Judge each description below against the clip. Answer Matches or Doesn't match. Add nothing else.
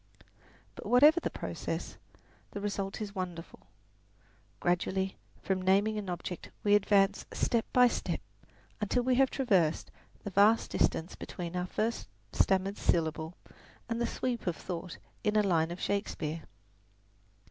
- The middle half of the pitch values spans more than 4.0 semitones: Doesn't match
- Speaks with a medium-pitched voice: Doesn't match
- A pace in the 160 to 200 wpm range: Doesn't match